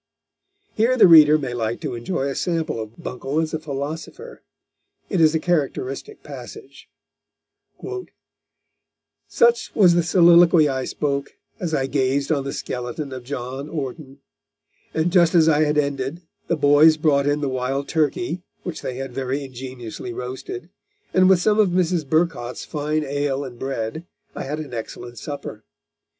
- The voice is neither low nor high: Yes, medium, 145 Hz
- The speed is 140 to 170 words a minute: Yes, average, 155 wpm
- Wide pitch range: No, average, 3.9 semitones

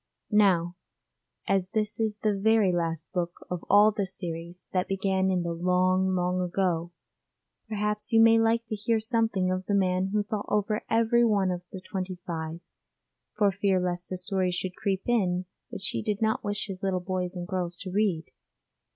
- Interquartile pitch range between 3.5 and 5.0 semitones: No, average, 2.7 semitones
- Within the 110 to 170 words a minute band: No, average, 185 wpm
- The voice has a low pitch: No, high, 190 Hz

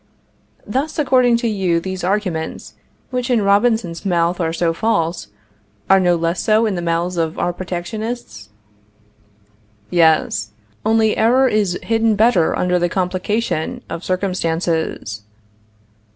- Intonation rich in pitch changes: No, average, 4.7 semitones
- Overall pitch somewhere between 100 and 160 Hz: No, medium, 185 Hz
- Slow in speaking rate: Yes, slow, 125 wpm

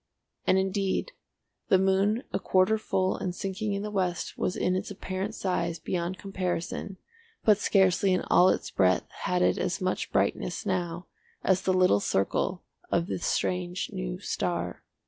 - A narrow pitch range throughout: Yes, narrow, 1.5 semitones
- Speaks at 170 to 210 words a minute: No, average, 160 wpm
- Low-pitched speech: No, medium, 185 Hz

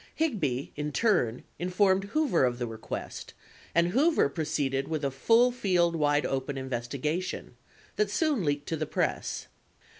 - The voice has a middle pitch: Yes, medium, 160 Hz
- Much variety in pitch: Yes, wide, 6.8 semitones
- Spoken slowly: No, average, 145 wpm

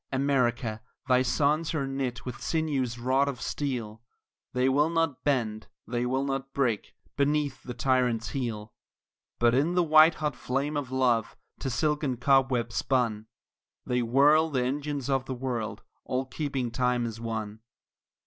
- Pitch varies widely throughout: No, average, 2.8 semitones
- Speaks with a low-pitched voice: Yes, low, 130 Hz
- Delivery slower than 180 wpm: Yes, average, 150 wpm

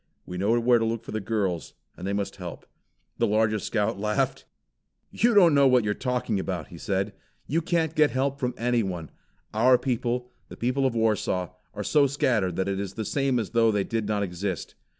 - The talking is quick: Yes, fast, 210 wpm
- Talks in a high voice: No, low, 110 Hz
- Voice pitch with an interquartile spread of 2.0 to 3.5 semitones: No, average, 4.2 semitones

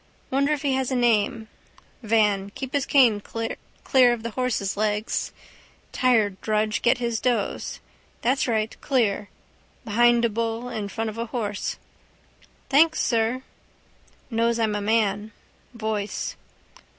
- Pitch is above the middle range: Yes, high, 230 Hz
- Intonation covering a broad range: No, narrow, 2.6 semitones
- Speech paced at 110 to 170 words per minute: Yes, slow, 135 wpm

